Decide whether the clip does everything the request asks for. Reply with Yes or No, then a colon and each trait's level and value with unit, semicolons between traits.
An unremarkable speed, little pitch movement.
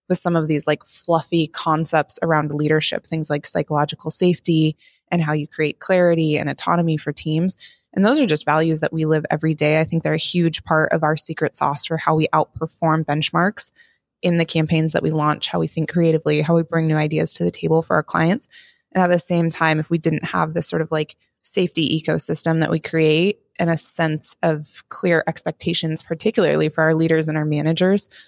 No: fast, 210 wpm; narrow, 1.6 semitones